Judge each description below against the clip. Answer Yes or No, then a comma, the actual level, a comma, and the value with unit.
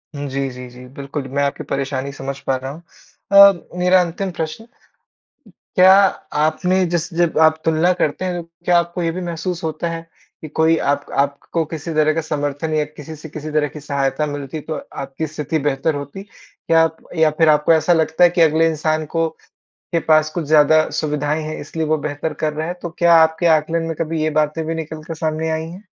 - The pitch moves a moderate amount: No, narrow, 2.0 semitones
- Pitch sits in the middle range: Yes, medium, 155 Hz